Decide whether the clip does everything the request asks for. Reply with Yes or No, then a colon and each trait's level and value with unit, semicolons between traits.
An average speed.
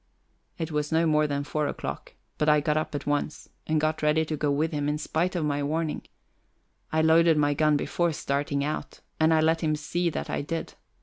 No: fast, 220 wpm